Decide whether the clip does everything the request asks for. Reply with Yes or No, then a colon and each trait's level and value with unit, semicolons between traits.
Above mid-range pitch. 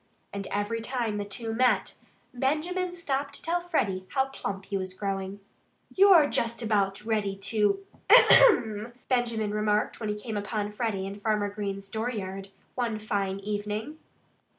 Yes: high, 215 Hz